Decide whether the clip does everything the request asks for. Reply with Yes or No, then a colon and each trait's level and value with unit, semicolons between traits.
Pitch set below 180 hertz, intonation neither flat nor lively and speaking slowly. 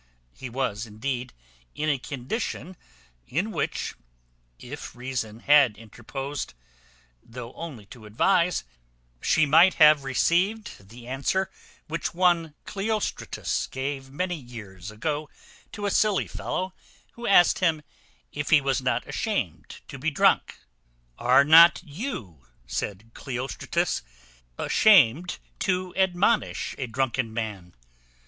No: medium, 140 Hz; wide, 6.5 semitones; slow, 115 wpm